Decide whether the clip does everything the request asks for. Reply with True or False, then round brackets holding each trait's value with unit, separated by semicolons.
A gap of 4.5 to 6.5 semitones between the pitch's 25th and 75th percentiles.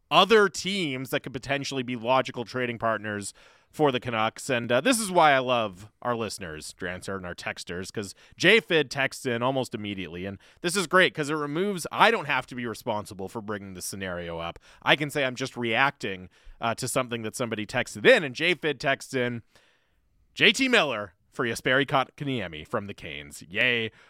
True (5.3 semitones)